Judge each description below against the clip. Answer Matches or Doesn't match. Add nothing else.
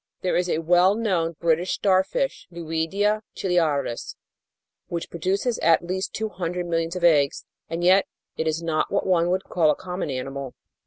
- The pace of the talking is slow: Doesn't match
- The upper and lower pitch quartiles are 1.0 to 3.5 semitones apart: Matches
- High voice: Doesn't match